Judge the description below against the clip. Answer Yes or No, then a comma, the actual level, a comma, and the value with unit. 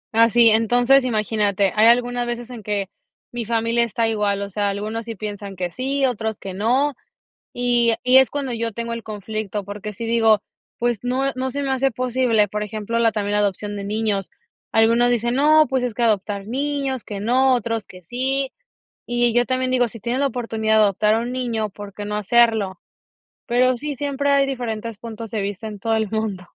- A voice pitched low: No, high, 230 Hz